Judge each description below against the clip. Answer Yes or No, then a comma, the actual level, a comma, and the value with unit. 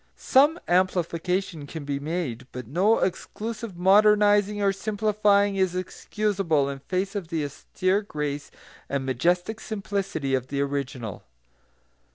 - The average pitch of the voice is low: No, medium, 185 Hz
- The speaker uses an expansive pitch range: Yes, wide, 6.1 semitones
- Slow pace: Yes, slow, 125 wpm